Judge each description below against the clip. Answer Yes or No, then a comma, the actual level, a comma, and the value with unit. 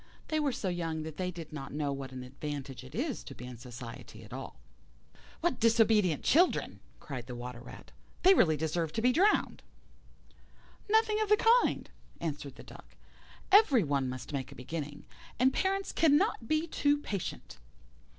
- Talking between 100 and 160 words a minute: No, average, 175 wpm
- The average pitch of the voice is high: No, medium, 165 Hz